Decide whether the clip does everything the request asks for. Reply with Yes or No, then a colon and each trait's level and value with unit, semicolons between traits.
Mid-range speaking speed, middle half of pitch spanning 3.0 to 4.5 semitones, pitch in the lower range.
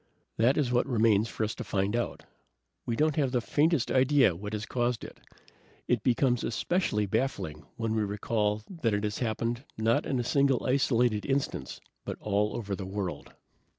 Yes: average, 180 wpm; average, 3.5 semitones; low, 115 Hz